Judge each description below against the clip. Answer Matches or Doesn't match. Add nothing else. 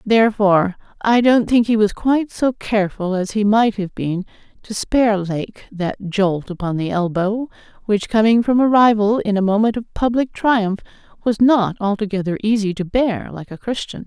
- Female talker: Matches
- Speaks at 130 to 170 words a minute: Doesn't match